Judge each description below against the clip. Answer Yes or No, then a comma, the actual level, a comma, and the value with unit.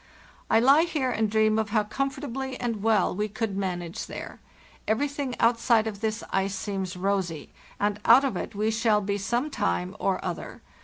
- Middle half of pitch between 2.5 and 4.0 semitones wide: Yes, average, 3.6 semitones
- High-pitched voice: Yes, high, 220 Hz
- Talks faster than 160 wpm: Yes, average, 175 wpm